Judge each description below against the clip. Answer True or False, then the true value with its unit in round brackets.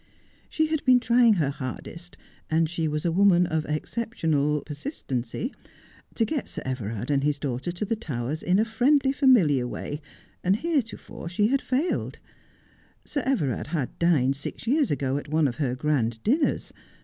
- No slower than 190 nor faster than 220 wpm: False (175 wpm)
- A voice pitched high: False (165 Hz)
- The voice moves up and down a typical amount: False (8.8 semitones)